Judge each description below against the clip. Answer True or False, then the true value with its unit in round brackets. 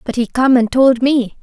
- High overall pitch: True (250 Hz)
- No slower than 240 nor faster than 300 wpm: True (255 wpm)